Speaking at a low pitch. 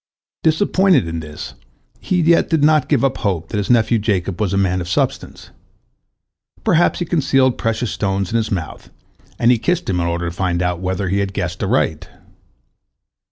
Yes: low, 100 Hz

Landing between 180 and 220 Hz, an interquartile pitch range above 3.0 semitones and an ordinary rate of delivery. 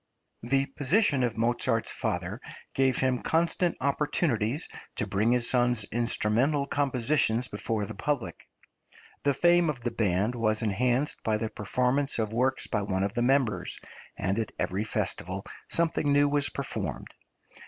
No: low, 125 Hz; average, 4.3 semitones; average, 145 wpm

